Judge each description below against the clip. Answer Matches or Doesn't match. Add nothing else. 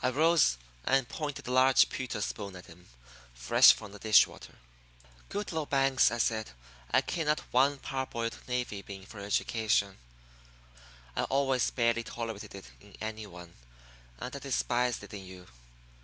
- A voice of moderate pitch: Doesn't match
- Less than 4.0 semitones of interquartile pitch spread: Doesn't match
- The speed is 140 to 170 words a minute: Matches